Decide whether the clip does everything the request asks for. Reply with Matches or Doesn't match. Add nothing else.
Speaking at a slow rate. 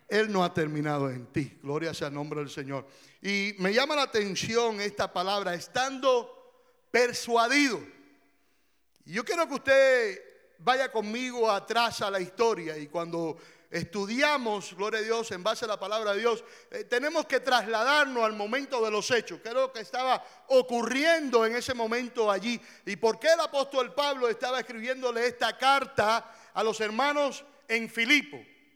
Doesn't match